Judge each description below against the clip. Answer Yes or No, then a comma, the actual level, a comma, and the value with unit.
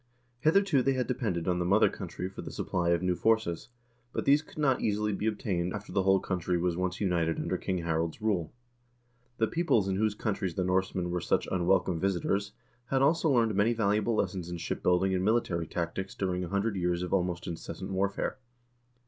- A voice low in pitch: Yes, very low, 95 Hz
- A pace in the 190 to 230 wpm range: Yes, average, 200 wpm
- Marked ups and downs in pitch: No, average, 3.6 semitones